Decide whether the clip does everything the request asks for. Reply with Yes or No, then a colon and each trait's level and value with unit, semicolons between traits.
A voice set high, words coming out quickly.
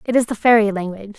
Yes: high, 215 Hz; fast, 255 wpm